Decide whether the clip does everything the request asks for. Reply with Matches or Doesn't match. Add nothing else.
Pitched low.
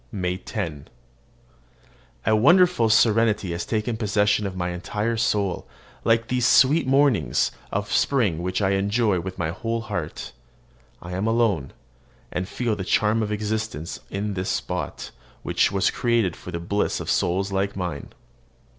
Matches